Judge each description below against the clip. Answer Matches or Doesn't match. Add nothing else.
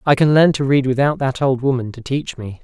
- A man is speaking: Matches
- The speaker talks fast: Matches